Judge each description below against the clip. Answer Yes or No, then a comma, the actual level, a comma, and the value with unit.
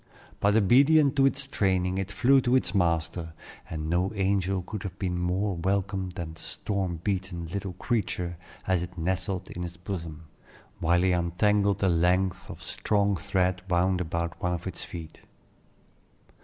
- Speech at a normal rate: Yes, average, 160 wpm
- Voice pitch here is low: Yes, very low, 95 Hz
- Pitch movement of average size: No, narrow, 2.3 semitones